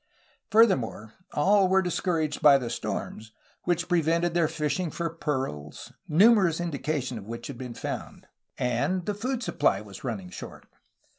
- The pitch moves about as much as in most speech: No, wide, 6.5 semitones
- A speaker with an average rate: Yes, average, 150 wpm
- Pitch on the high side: No, medium, 155 Hz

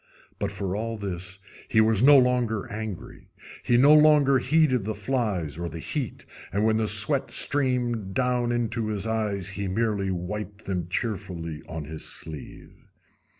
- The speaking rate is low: No, average, 155 wpm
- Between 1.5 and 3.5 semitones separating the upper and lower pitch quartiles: No, average, 4.5 semitones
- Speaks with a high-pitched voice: No, low, 110 Hz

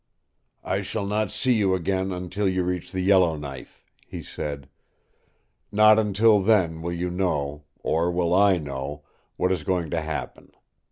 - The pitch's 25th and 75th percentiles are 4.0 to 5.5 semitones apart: No, average, 3.5 semitones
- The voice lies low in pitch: Yes, very low, 90 Hz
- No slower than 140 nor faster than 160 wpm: Yes, average, 155 wpm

